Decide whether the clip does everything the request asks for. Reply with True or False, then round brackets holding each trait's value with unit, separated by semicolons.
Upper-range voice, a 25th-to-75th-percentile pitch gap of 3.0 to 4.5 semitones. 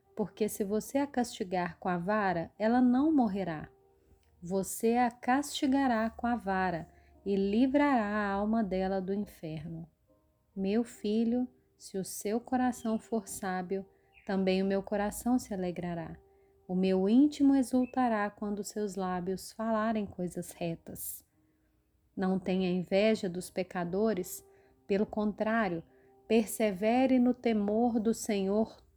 True (210 Hz; 3.7 semitones)